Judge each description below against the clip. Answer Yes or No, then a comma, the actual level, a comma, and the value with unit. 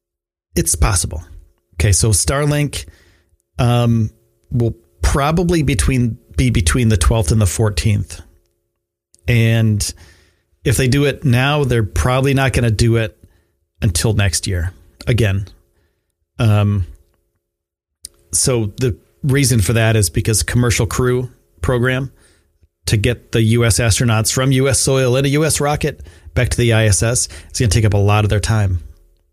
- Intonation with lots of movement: Yes, wide, 6.1 semitones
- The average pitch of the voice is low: Yes, low, 110 Hz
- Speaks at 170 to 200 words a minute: No, average, 145 wpm